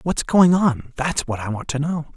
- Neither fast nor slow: No, fast, 250 wpm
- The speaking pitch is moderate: Yes, medium, 145 Hz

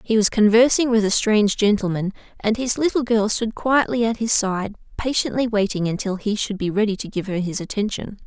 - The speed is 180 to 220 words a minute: Yes, fast, 205 wpm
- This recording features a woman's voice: Yes, female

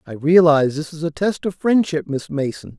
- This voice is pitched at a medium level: Yes, medium, 160 Hz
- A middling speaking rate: No, fast, 215 wpm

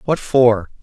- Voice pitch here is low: Yes, low, 120 Hz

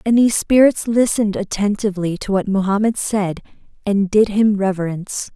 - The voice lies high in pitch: Yes, high, 205 Hz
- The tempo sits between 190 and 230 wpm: No, average, 145 wpm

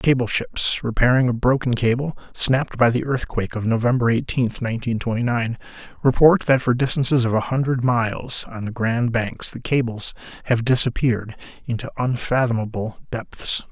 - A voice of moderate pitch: No, low, 120 Hz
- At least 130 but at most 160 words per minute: Yes, average, 155 wpm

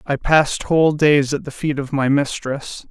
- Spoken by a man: Yes, male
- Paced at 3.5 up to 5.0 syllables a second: Yes, 4.7 syllables/s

